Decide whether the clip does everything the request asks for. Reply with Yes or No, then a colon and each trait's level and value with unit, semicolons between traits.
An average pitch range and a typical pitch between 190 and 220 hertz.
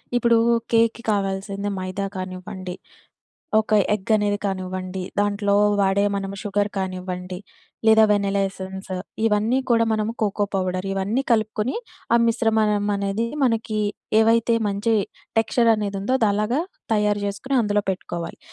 No: narrow, 2.3 semitones; high, 205 Hz